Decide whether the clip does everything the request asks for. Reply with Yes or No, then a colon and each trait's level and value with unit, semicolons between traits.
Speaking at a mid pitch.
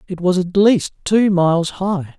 Yes: medium, 180 Hz